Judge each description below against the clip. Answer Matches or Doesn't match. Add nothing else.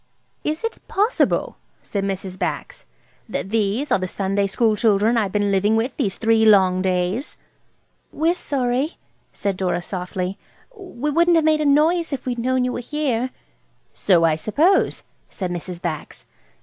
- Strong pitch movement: Matches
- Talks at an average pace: Matches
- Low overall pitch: Doesn't match